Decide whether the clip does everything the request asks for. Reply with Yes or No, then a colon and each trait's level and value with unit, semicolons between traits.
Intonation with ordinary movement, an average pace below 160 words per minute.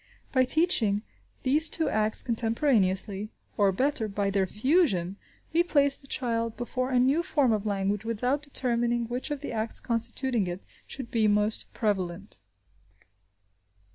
Yes: average, 4.4 semitones; average, 140 wpm